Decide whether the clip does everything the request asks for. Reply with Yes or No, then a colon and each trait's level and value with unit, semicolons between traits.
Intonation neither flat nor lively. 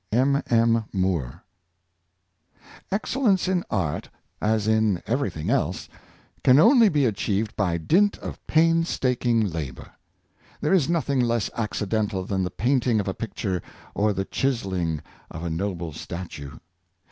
No: wide, 6.6 semitones